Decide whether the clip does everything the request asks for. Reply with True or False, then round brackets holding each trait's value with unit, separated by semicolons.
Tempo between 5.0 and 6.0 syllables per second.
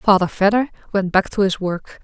True (5.2 syllables/s)